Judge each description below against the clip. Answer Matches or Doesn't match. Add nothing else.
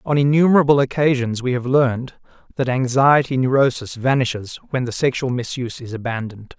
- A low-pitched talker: Matches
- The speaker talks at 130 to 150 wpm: Matches